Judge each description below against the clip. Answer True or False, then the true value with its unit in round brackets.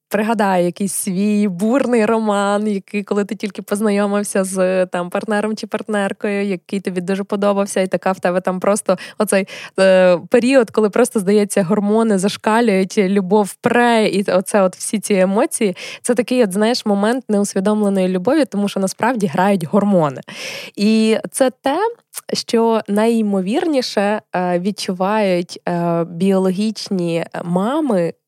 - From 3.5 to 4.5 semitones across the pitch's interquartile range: False (2.6 semitones)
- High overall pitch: True (205 Hz)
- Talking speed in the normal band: True (130 wpm)